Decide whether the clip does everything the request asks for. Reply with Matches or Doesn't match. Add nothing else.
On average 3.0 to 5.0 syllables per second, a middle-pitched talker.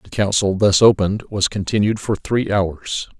Doesn't match